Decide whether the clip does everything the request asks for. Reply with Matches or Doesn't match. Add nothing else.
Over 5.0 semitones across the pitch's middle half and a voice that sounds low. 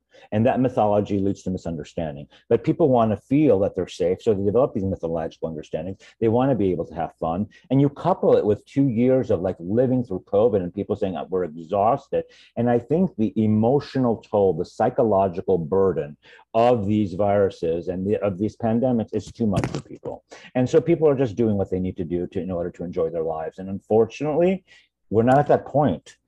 Matches